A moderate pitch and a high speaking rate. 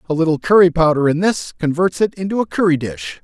Yes: medium, 165 Hz; fast, 225 wpm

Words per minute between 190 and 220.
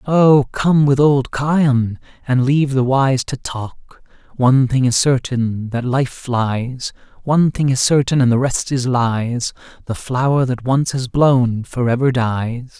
No: average, 170 wpm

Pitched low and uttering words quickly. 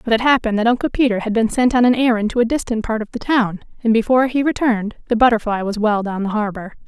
No: high, 225 Hz; fast, 260 wpm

